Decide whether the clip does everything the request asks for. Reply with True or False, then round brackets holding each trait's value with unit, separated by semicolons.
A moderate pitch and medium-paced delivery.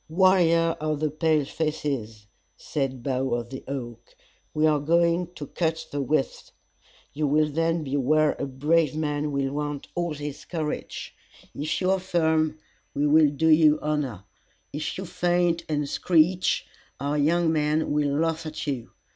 True (155 Hz; 160 wpm)